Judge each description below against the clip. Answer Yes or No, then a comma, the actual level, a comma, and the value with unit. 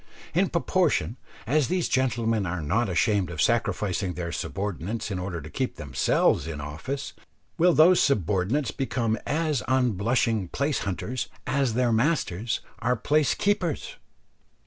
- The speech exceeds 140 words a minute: No, slow, 135 wpm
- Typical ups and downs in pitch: No, wide, 6.8 semitones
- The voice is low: Yes, low, 115 Hz